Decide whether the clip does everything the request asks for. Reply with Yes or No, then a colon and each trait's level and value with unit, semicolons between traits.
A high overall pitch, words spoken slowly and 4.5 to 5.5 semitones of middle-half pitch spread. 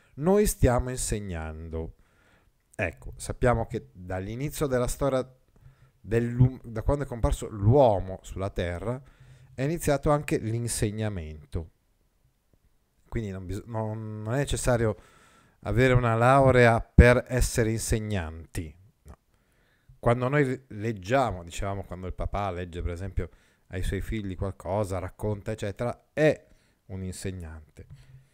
No: low, 110 Hz; slow, 110 wpm; average, 5.1 semitones